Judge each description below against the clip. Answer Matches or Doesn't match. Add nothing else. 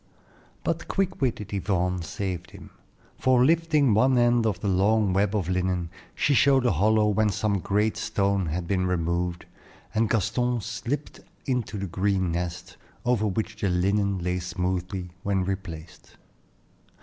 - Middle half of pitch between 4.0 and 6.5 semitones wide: Doesn't match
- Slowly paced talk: Doesn't match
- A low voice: Matches